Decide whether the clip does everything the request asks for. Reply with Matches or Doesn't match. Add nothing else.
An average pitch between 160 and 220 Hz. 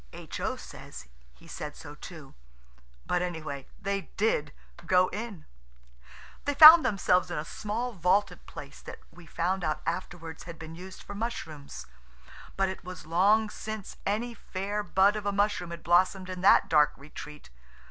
Matches